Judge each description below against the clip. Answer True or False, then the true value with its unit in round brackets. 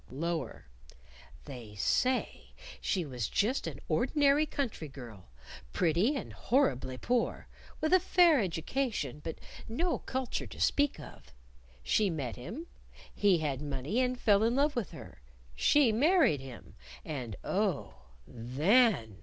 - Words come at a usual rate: False (130 wpm)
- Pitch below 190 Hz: False (195 Hz)